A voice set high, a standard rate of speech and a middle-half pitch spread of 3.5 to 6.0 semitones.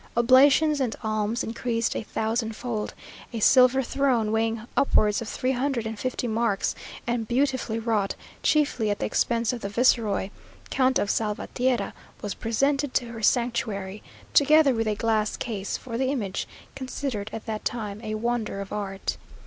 No: high, 230 Hz; average, 160 wpm; average, 3.1 semitones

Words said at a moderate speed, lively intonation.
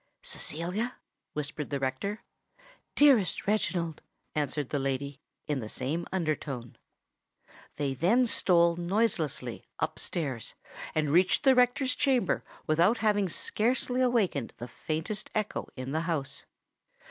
No: slow, 125 wpm; wide, 6.9 semitones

